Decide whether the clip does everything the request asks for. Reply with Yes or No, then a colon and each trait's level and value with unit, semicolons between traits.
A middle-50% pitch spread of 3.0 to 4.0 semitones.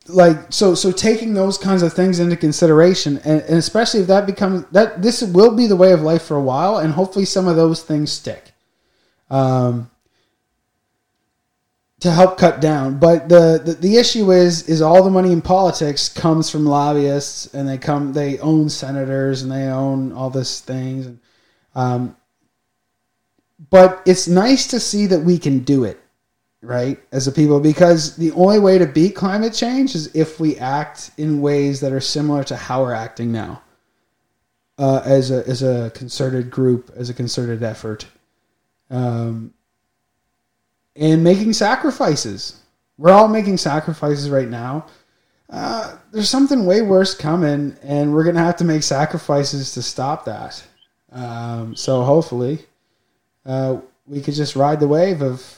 No: average, 5.3 semitones